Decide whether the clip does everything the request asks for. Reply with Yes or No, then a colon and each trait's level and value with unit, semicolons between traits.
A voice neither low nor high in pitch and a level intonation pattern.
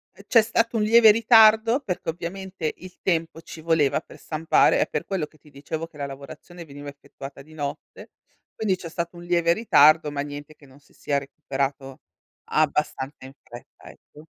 No: medium, 160 Hz; average, 4.5 semitones